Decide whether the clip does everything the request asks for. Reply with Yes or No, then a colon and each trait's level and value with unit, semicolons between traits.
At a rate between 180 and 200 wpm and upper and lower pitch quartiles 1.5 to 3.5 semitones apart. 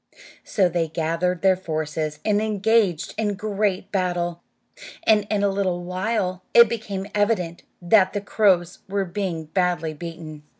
No: average, 145 wpm; average, 3.2 semitones